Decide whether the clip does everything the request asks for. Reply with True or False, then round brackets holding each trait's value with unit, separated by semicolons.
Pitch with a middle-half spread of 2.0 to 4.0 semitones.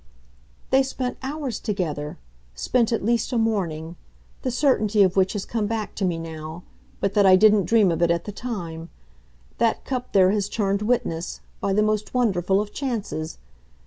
False (4.7 semitones)